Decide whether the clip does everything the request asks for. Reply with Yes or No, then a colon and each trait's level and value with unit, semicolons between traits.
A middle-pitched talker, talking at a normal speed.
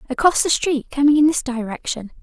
No: very high, 270 Hz; average, 190 wpm